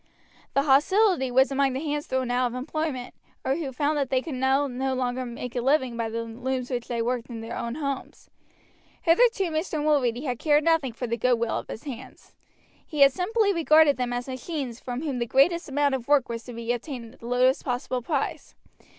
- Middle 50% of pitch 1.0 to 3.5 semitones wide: Yes, average, 3.2 semitones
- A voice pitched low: No, very high, 260 Hz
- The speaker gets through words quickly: Yes, fast, 210 wpm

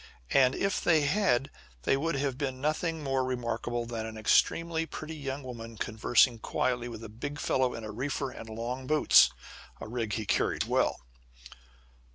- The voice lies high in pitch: No, low, 130 Hz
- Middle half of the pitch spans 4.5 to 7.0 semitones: No, average, 3.9 semitones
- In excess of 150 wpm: Yes, average, 170 wpm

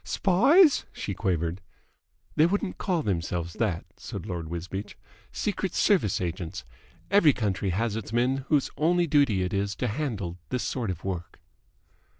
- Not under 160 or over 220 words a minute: No, average, 150 wpm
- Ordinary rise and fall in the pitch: No, wide, 8.7 semitones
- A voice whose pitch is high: No, low, 105 Hz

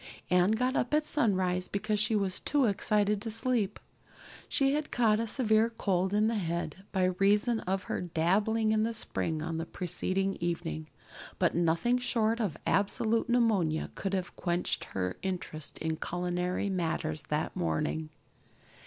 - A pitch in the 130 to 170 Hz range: No, high, 195 Hz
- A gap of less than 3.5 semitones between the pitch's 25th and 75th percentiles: No, average, 4.3 semitones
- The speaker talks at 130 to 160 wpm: Yes, average, 155 wpm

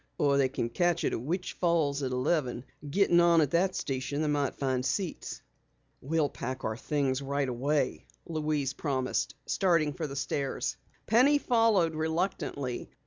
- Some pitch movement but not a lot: Yes, average, 4.1 semitones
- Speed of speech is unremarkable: Yes, average, 155 wpm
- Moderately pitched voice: Yes, medium, 145 Hz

